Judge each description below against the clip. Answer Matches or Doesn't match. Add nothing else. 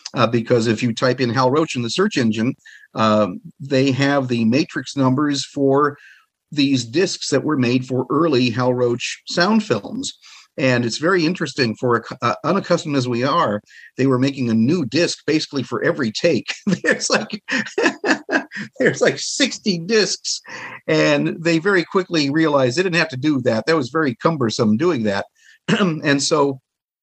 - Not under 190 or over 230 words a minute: Doesn't match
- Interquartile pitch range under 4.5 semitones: Doesn't match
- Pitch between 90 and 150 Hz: Matches